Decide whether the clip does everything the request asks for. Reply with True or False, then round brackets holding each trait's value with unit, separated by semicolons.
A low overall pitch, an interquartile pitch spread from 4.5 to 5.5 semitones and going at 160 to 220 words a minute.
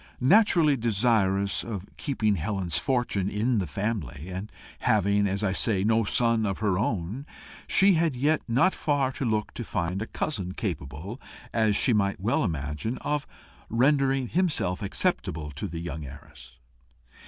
False (105 Hz; 5.1 semitones; 150 wpm)